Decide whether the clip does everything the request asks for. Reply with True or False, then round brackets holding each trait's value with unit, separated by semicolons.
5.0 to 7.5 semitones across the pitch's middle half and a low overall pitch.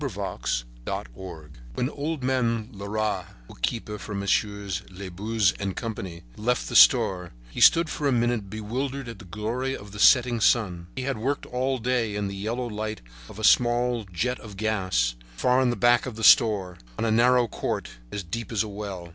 False (3.9 semitones; 110 Hz)